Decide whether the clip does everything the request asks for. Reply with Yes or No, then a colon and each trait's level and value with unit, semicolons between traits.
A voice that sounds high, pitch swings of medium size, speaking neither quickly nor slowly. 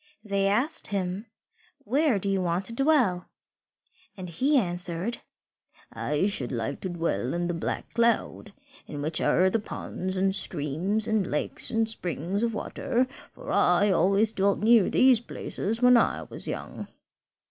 Yes: high, 195 Hz; average, 4.5 semitones; average, 155 wpm